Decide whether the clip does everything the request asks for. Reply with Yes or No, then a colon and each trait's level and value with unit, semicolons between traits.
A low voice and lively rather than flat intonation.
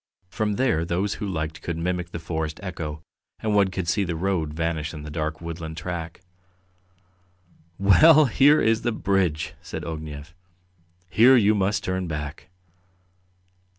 No: very low, 85 Hz; average, 4.2 semitones